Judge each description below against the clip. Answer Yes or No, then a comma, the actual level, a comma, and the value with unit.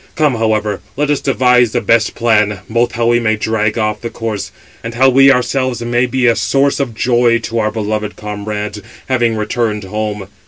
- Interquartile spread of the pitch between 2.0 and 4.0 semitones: Yes, narrow, 2.4 semitones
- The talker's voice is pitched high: No, low, 115 Hz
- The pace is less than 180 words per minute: No, average, 190 wpm